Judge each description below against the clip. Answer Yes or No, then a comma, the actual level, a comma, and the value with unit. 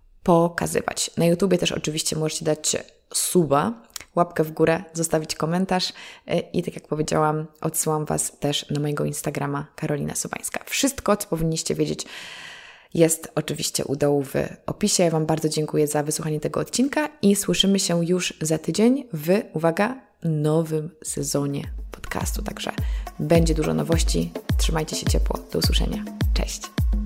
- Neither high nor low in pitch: Yes, medium, 160 Hz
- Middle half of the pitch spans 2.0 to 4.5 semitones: Yes, average, 3.2 semitones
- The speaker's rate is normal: Yes, average, 140 wpm